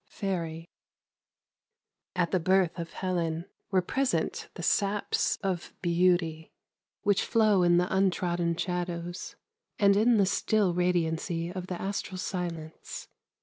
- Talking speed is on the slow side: Yes, slow, 125 wpm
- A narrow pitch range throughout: Yes, narrow, 2.2 semitones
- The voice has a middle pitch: Yes, medium, 180 Hz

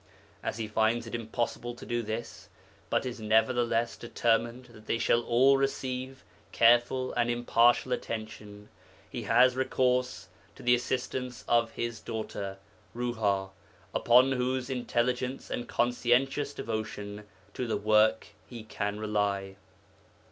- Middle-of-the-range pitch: No, low, 120 Hz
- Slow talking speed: Yes, slow, 125 wpm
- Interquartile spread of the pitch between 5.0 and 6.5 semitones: No, narrow, 2.4 semitones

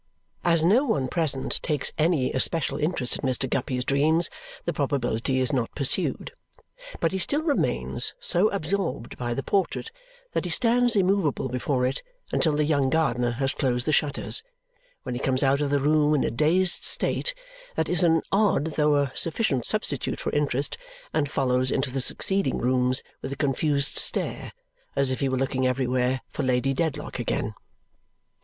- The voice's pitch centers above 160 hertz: No, medium, 140 Hz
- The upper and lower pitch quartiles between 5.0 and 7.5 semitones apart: No, average, 4.1 semitones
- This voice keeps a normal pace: Yes, average, 170 wpm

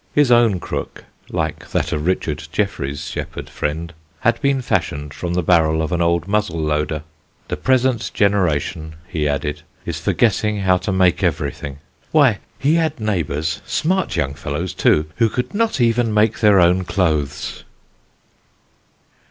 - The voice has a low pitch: Yes, very low, 90 Hz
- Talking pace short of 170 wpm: Yes, average, 150 wpm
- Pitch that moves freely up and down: Yes, wide, 6.3 semitones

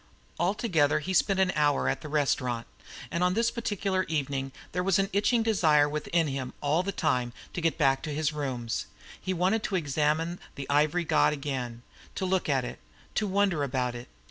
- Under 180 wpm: No, average, 190 wpm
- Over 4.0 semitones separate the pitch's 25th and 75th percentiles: Yes, average, 5.2 semitones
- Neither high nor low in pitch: Yes, medium, 155 Hz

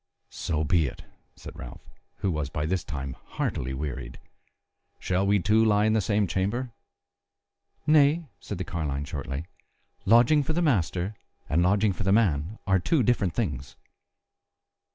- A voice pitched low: Yes, very low, 95 Hz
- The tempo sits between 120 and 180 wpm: Yes, average, 155 wpm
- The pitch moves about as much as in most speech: No, wide, 6.5 semitones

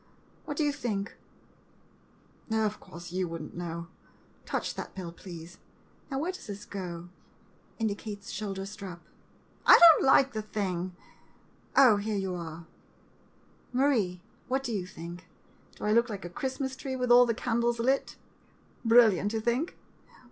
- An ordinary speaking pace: Yes, average, 160 wpm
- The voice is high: Yes, high, 210 Hz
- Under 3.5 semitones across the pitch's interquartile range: No, average, 5.3 semitones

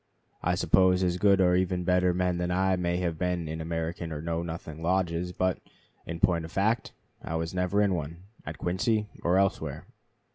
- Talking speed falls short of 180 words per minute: No, average, 190 wpm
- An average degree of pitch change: No, narrow, 1.7 semitones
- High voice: No, very low, 90 Hz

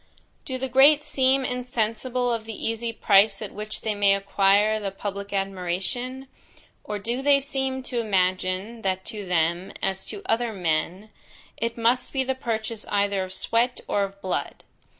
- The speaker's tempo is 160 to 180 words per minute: Yes, average, 165 wpm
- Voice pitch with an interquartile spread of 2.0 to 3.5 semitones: No, average, 4.1 semitones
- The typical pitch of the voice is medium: No, high, 215 Hz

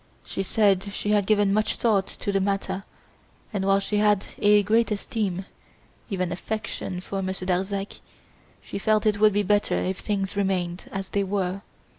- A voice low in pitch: No, high, 200 Hz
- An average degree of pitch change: No, narrow, 1.5 semitones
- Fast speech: No, average, 170 wpm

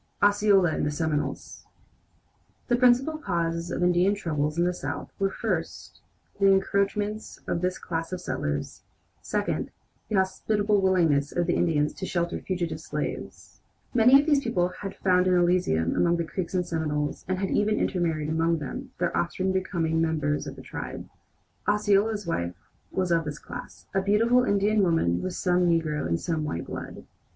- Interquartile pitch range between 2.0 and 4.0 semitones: Yes, average, 3.6 semitones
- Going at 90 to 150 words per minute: No, average, 165 wpm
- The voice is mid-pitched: Yes, medium, 180 Hz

